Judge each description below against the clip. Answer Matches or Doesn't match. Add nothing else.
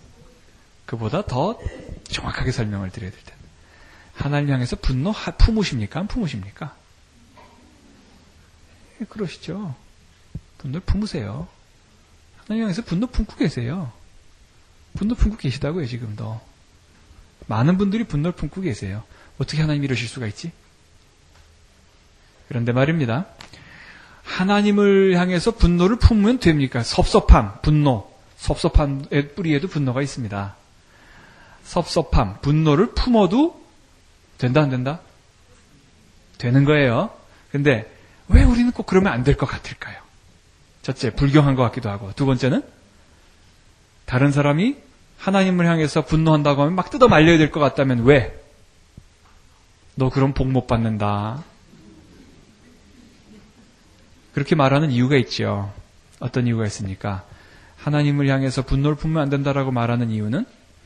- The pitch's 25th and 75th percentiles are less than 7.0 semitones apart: Doesn't match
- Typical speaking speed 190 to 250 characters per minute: Doesn't match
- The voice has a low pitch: Matches